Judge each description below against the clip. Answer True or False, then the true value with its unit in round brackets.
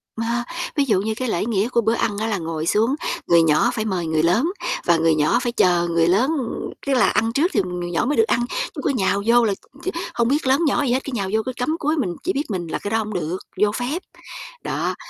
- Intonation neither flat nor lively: False (6.2 semitones)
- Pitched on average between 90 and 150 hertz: False (220 Hz)